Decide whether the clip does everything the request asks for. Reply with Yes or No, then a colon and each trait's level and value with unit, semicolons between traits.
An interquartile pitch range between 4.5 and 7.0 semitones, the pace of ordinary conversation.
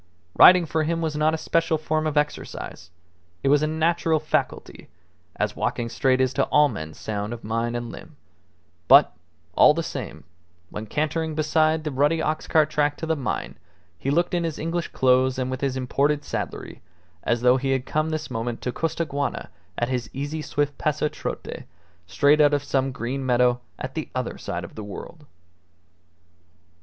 No: average, 3.7 semitones; average, 180 wpm